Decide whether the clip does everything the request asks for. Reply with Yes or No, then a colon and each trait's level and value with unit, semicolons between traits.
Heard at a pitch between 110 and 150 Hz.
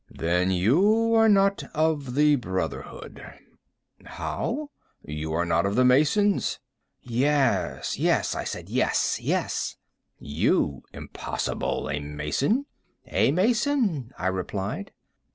Yes: low, 135 Hz